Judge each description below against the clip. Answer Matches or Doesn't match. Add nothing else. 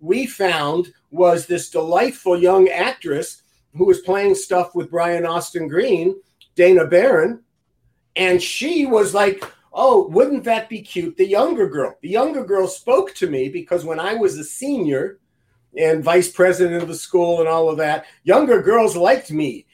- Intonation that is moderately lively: Doesn't match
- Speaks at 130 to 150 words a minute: Doesn't match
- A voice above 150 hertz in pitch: Matches